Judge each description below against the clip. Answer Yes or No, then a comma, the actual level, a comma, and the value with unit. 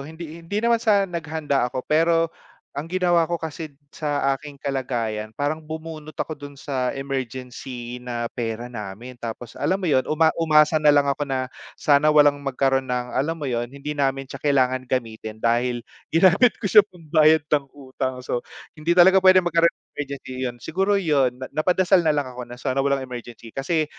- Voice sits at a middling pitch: Yes, medium, 145 Hz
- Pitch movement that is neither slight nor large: Yes, average, 4.1 semitones